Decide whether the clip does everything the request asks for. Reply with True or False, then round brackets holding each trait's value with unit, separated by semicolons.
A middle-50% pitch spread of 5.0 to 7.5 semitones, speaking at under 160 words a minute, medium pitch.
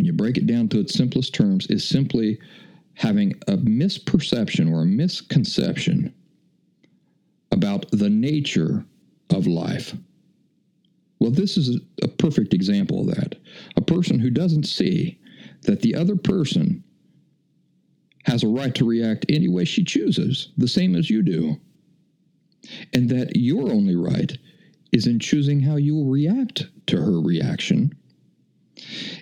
True (5.5 semitones; 140 wpm; 175 Hz)